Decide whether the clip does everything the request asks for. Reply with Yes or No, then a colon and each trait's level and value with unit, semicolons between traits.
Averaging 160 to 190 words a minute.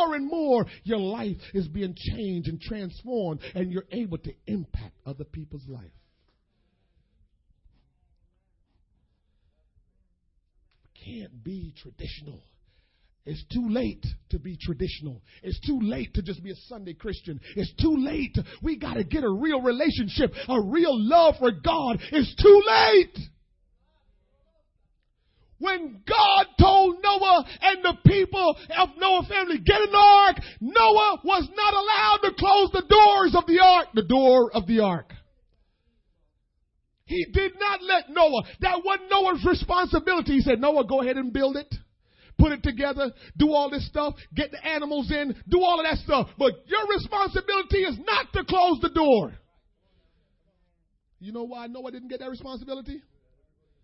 No: average, 145 wpm